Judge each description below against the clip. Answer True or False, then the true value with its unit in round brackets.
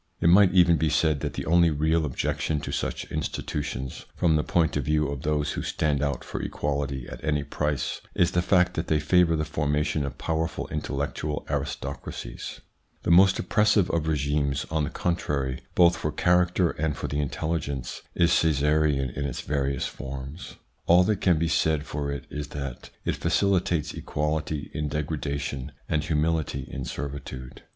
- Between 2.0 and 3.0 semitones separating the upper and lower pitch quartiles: True (2.6 semitones)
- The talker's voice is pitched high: False (75 Hz)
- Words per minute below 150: False (175 wpm)